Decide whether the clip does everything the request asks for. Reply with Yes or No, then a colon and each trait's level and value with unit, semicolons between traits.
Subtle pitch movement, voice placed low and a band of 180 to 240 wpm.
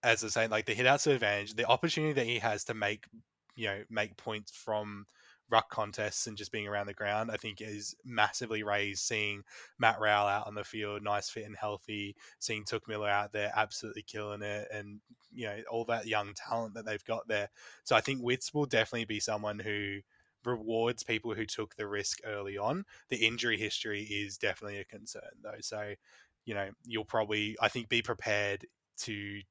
Yes: narrow, 1.8 semitones; low, 105 Hz; average, 200 wpm